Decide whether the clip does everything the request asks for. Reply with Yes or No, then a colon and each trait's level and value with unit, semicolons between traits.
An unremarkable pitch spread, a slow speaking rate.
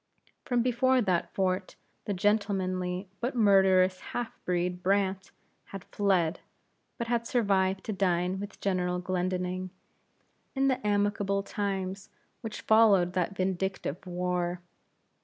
No: narrow, 2.2 semitones; slow, 120 wpm